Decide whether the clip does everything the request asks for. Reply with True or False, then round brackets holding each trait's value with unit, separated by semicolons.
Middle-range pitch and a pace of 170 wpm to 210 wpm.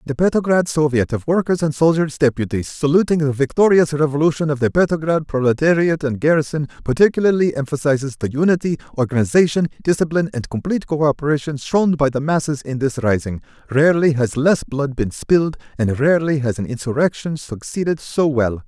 False (145 Hz; 155 wpm)